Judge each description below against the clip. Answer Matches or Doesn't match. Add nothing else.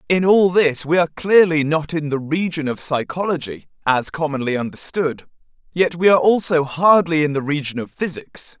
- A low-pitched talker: Doesn't match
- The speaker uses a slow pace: Doesn't match